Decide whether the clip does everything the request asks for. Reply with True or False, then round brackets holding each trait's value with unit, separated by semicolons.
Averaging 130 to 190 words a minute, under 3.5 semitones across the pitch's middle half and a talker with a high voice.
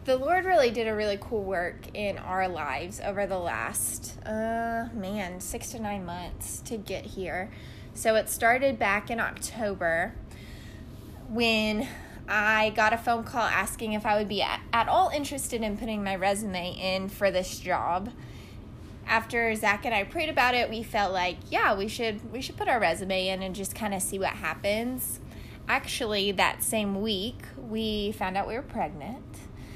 True (175 wpm; 2.9 semitones; 210 Hz)